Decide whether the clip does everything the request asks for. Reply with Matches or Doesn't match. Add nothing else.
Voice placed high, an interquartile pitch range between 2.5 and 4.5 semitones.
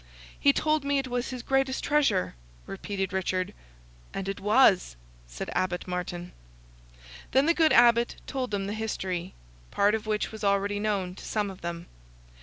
Doesn't match